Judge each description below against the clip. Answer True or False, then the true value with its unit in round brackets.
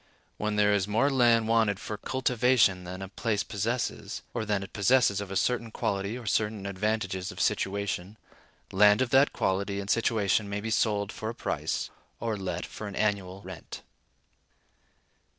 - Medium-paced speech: True (170 wpm)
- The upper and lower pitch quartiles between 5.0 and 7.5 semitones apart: False (2.5 semitones)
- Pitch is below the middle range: True (105 Hz)